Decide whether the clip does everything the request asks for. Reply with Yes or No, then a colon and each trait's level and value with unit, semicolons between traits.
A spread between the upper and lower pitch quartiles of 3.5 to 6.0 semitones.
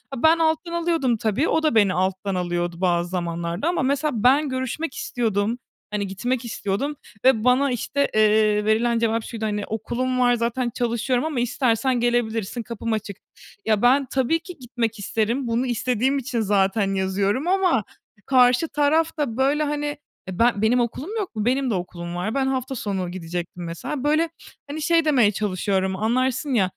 Yes: average, 4.8 semitones